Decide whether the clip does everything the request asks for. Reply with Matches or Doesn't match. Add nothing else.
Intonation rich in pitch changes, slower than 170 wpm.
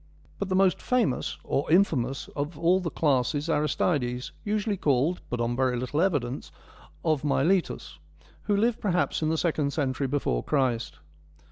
Matches